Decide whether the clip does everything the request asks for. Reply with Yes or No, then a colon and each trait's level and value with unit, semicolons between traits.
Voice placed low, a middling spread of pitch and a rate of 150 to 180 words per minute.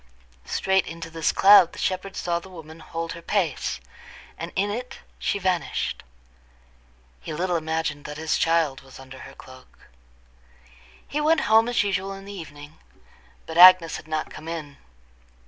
No: medium, 170 Hz; average, 3.4 semitones; average, 160 wpm